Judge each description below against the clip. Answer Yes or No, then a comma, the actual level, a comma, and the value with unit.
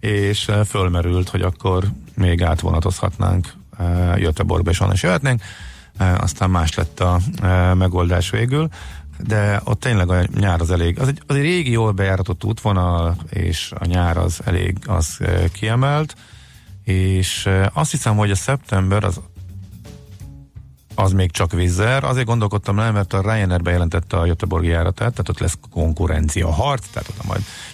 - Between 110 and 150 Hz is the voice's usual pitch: No, very low, 95 Hz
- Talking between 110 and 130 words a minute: No, average, 145 wpm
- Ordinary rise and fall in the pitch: Yes, average, 3.3 semitones